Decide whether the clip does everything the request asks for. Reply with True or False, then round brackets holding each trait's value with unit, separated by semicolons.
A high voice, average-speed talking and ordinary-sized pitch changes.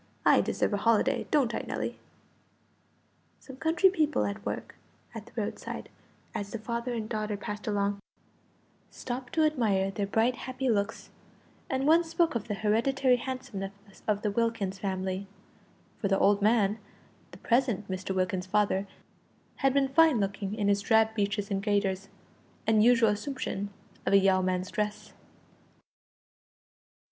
True (210 Hz; 145 wpm; 3.7 semitones)